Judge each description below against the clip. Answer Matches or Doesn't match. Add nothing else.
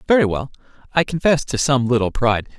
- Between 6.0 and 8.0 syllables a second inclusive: Matches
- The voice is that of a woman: Doesn't match